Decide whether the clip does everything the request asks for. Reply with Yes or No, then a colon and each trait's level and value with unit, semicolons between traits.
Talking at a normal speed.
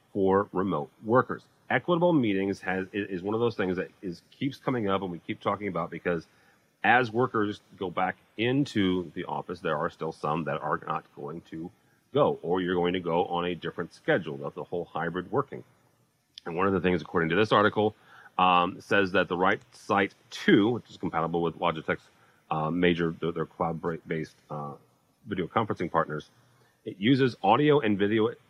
Yes: average, 185 wpm